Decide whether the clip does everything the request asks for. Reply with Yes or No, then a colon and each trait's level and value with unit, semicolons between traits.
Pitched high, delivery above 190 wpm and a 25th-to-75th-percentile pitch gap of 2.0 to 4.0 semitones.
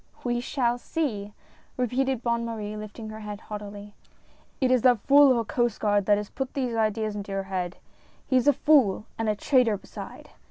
Yes: high, 225 Hz; fast, 205 wpm; average, 3.5 semitones